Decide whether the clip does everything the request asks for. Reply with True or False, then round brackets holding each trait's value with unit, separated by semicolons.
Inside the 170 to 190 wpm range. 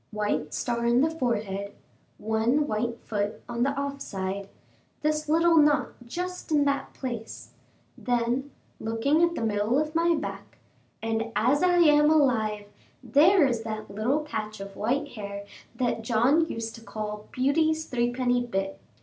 False (150 wpm)